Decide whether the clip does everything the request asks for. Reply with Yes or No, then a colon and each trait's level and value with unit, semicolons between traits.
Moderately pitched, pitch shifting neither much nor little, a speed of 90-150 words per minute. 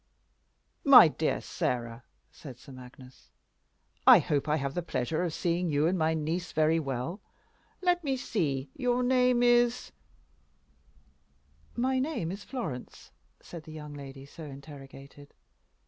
No: medium, 155 Hz; wide, 5.8 semitones; average, 140 wpm